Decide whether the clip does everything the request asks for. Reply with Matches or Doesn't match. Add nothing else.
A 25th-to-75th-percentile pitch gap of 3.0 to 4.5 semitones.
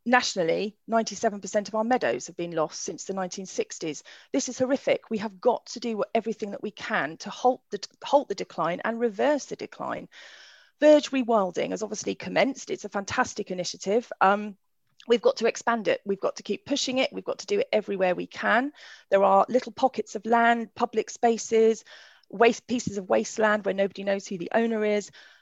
Matches